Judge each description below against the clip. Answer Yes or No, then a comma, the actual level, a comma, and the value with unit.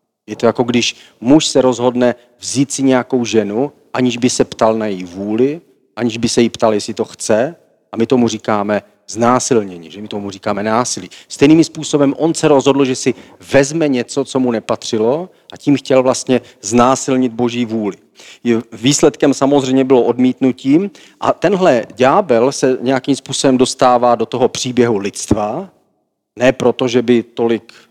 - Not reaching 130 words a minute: No, average, 160 wpm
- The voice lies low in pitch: Yes, low, 125 Hz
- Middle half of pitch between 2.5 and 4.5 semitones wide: Yes, average, 2.8 semitones